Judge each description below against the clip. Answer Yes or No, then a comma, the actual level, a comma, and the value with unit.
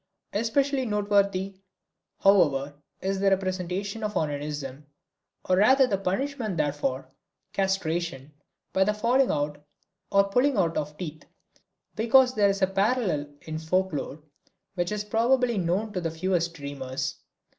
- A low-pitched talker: No, high, 190 Hz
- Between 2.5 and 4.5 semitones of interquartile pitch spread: No, average, 4.9 semitones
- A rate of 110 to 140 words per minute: Yes, slow, 135 wpm